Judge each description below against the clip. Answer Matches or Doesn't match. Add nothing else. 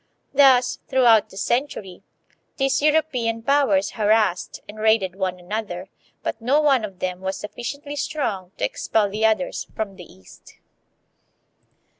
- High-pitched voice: Matches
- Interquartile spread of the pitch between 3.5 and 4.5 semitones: Doesn't match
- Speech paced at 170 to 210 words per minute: Doesn't match